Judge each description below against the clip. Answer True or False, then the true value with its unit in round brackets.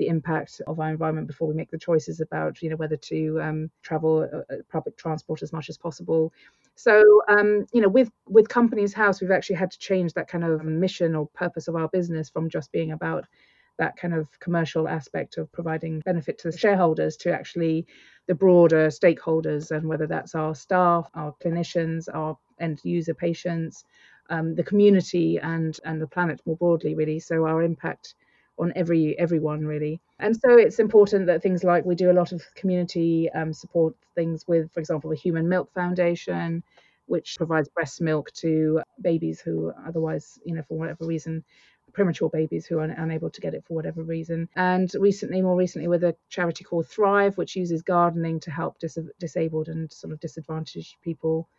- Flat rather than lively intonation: True (1.9 semitones)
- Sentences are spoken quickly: False (190 wpm)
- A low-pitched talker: False (165 Hz)